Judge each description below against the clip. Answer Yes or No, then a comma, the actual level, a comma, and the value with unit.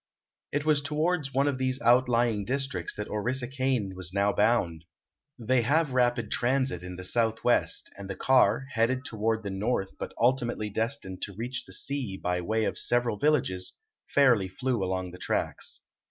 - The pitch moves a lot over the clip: No, average, 4.6 semitones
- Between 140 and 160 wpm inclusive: No, average, 170 wpm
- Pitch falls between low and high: No, low, 120 Hz